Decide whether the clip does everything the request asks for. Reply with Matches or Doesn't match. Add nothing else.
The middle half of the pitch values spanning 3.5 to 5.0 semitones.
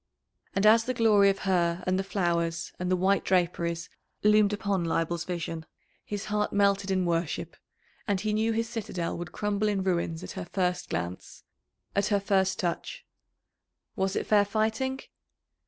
Doesn't match